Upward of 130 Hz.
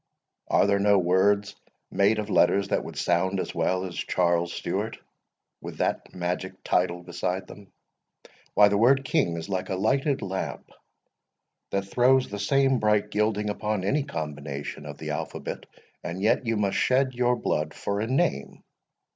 No: low, 100 Hz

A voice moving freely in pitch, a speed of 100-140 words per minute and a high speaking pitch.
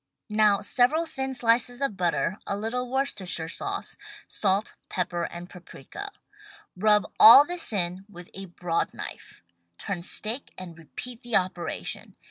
Yes: wide, 5.7 semitones; slow, 135 wpm; high, 205 Hz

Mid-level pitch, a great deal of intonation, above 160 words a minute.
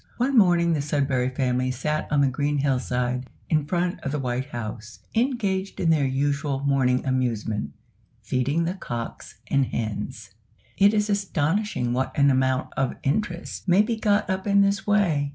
Yes: medium, 145 Hz; wide, 6.7 semitones; average, 170 wpm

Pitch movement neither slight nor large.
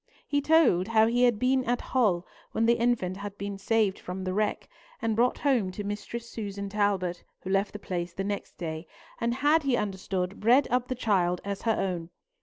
Yes: average, 3.9 semitones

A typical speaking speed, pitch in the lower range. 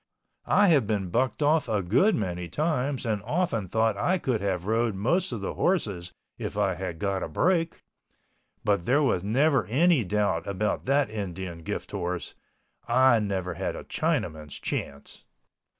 Yes: average, 160 wpm; low, 105 Hz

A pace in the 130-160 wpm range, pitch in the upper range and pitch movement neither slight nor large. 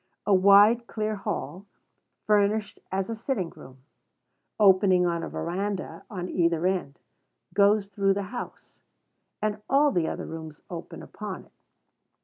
Yes: slow, 135 wpm; high, 195 Hz; average, 3.0 semitones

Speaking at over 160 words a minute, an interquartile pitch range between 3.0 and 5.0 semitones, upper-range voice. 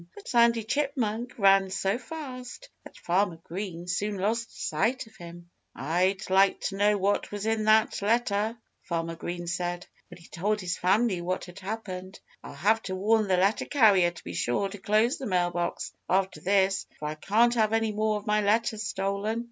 Yes: average, 190 wpm; average, 3.4 semitones; high, 200 Hz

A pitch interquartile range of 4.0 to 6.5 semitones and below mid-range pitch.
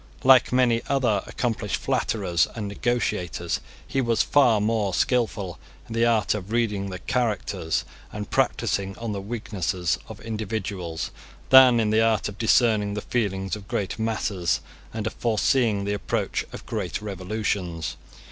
No: average, 3.0 semitones; low, 105 Hz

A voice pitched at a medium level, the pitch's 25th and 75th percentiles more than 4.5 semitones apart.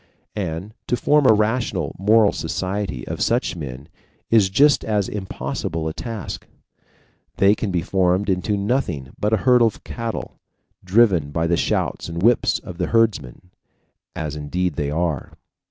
No: very low, 95 Hz; average, 5.1 semitones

